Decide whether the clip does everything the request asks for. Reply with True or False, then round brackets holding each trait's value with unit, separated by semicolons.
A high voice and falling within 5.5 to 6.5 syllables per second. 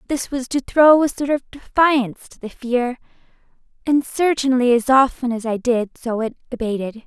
False (255 Hz; 4.8 syllables/s)